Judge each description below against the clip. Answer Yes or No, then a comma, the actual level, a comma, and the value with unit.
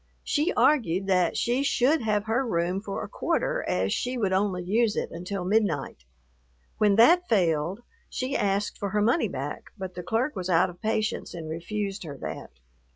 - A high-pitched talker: Yes, high, 200 Hz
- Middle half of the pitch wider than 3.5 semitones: Yes, average, 4.2 semitones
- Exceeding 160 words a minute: Yes, average, 180 wpm